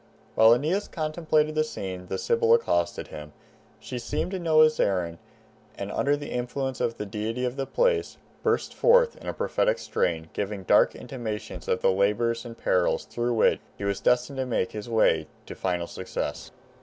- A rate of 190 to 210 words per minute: No, average, 180 wpm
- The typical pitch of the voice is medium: No, low, 120 Hz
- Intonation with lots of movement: Yes, wide, 7.6 semitones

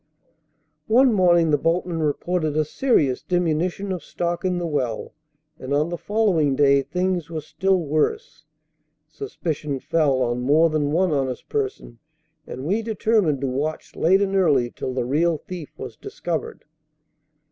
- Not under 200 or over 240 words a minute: No, average, 150 wpm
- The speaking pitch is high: No, medium, 165 Hz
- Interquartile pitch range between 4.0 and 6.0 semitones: Yes, average, 4.4 semitones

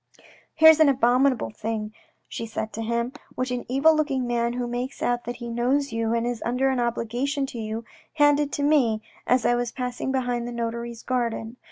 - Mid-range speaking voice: No, high, 245 Hz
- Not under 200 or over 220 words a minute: Yes, fast, 205 wpm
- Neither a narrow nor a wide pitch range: No, narrow, 2.2 semitones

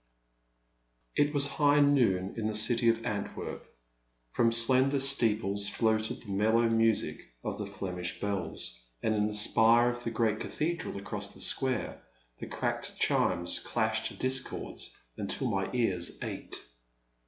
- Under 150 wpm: Yes, average, 140 wpm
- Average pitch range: Yes, average, 3.8 semitones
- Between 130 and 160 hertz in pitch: No, low, 115 Hz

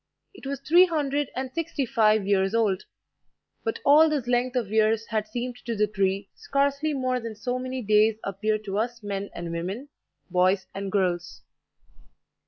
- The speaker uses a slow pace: No, average, 170 wpm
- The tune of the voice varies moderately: Yes, average, 4.5 semitones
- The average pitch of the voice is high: Yes, high, 225 Hz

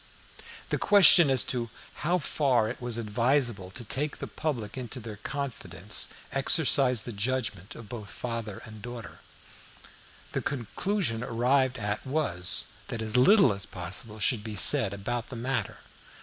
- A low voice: Yes, low, 120 Hz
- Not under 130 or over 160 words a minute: Yes, average, 150 wpm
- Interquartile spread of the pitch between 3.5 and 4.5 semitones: Yes, average, 4.0 semitones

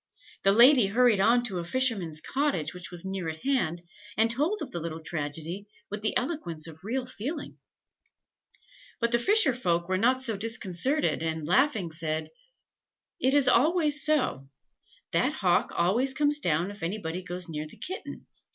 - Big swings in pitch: Yes, wide, 7.4 semitones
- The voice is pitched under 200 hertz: No, high, 205 Hz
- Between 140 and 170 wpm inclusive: Yes, average, 165 wpm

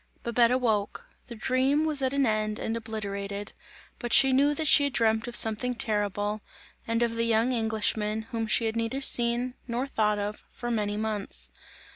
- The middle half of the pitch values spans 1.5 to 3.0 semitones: Yes, average, 2.7 semitones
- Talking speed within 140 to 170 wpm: No, average, 180 wpm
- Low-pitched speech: No, high, 230 Hz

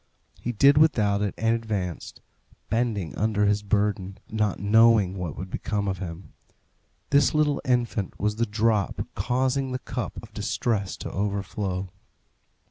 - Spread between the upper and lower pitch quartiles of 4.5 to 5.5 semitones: No, average, 3.0 semitones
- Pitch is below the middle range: Yes, low, 105 Hz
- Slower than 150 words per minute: Yes, average, 140 wpm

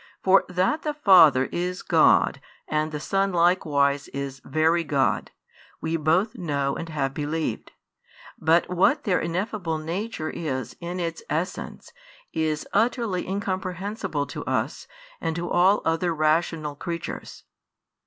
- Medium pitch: Yes, medium, 170 Hz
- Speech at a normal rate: No, slow, 130 wpm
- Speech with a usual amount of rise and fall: Yes, average, 3.3 semitones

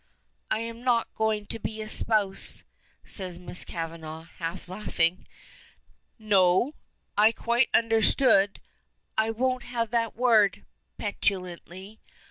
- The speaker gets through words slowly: Yes, slow, 105 wpm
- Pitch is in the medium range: No, high, 215 Hz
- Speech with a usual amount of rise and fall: Yes, average, 3.9 semitones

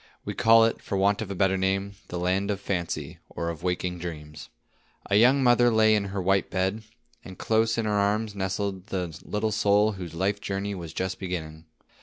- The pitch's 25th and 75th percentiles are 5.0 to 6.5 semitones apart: No, narrow, 2.4 semitones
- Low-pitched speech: Yes, low, 100 Hz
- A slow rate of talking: No, average, 200 wpm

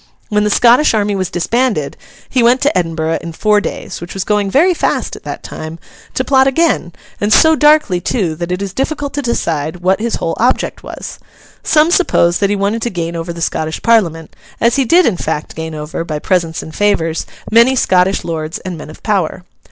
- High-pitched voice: Yes, high, 195 Hz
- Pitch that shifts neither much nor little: No, wide, 6.3 semitones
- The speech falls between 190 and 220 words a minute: Yes, average, 200 wpm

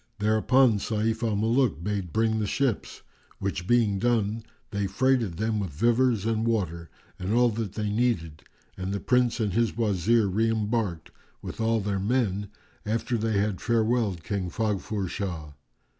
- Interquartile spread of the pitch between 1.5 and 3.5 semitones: Yes, average, 2.8 semitones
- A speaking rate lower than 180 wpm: Yes, average, 160 wpm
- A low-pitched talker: Yes, low, 110 Hz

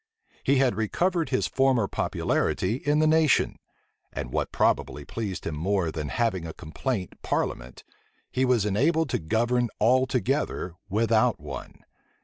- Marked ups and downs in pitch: Yes, wide, 6.3 semitones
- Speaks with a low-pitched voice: Yes, low, 115 Hz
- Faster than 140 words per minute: No, slow, 135 wpm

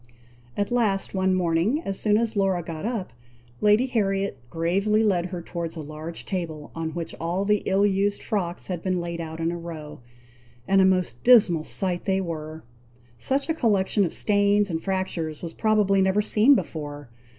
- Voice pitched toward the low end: No, high, 190 Hz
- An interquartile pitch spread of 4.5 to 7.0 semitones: No, average, 3.6 semitones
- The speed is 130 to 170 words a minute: No, average, 180 wpm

